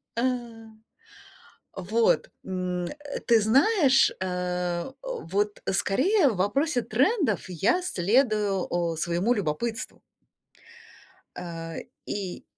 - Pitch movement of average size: No, wide, 6.2 semitones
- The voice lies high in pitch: Yes, high, 215 Hz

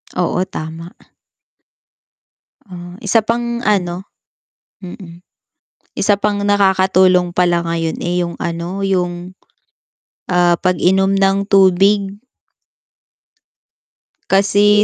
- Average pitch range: No, narrow, 2.2 semitones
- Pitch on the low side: No, high, 190 Hz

